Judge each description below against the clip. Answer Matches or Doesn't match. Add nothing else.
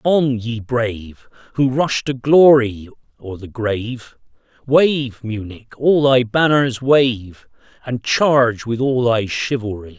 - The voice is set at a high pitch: Doesn't match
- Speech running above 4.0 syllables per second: Doesn't match